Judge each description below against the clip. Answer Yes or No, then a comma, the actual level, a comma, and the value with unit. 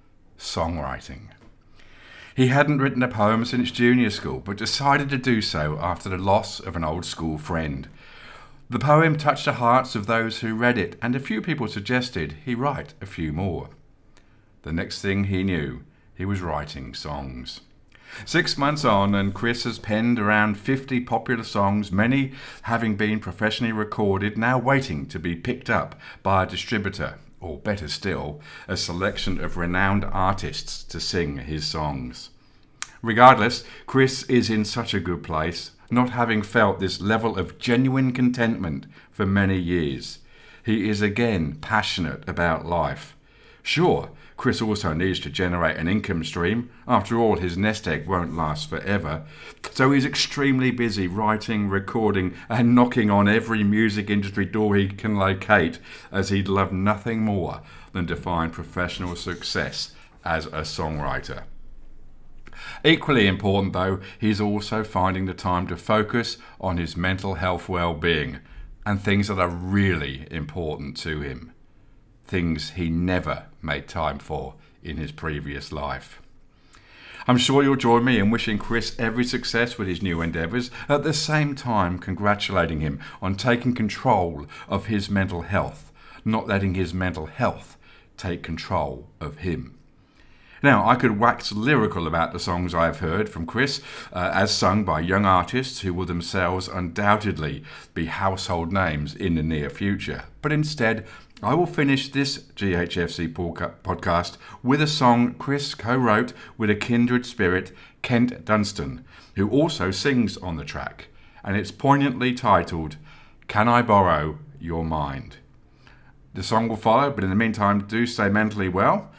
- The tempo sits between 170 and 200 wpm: No, average, 155 wpm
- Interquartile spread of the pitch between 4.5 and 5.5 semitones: Yes, average, 5.1 semitones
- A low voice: Yes, low, 100 Hz